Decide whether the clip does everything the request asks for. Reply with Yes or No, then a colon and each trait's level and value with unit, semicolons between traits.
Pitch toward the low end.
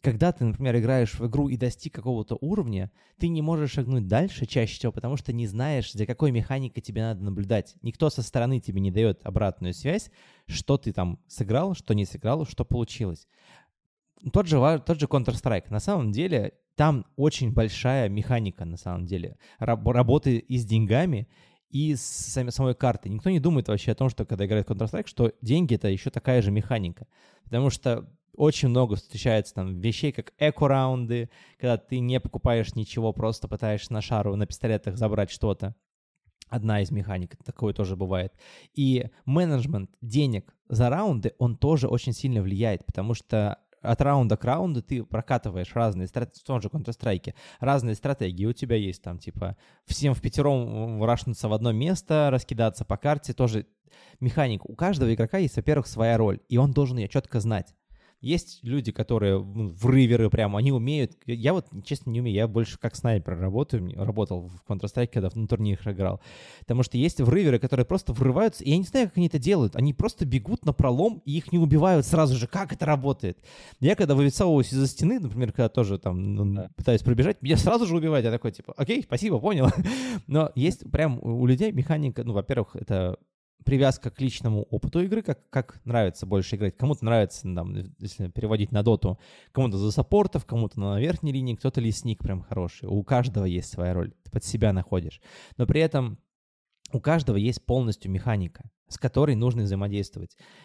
Yes: low, 120 Hz